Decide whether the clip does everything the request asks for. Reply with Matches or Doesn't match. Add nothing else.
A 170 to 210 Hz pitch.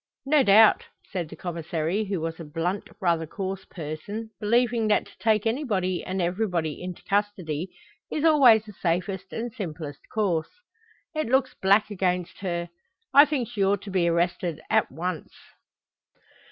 Matches